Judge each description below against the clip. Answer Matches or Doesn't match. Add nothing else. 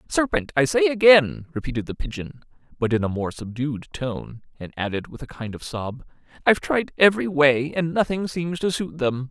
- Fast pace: Doesn't match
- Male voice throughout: Matches